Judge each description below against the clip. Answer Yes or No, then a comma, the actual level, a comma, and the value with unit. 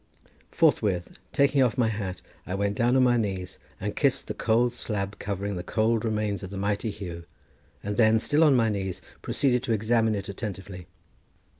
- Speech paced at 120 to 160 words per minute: No, average, 180 wpm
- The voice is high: No, low, 105 Hz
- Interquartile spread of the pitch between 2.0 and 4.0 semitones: Yes, average, 3.1 semitones